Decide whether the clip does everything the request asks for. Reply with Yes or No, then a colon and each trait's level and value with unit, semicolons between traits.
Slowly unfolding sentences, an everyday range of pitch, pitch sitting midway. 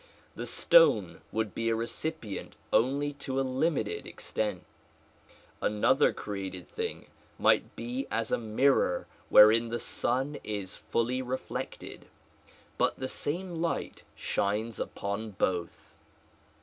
No: slow, 115 wpm; average, 4.1 semitones; low, 115 Hz